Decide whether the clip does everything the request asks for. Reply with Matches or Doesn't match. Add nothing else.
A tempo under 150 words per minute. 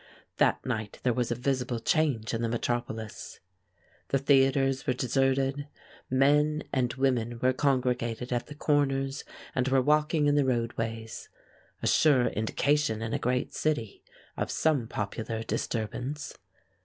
Matches